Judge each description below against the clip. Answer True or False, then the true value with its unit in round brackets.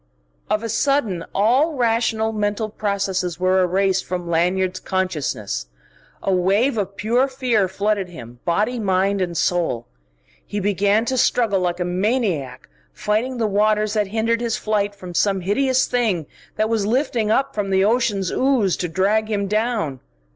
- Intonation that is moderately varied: True (3.3 semitones)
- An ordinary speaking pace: True (155 wpm)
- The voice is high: True (205 Hz)